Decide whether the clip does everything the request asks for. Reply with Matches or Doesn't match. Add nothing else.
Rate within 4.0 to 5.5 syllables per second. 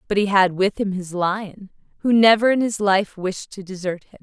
Matches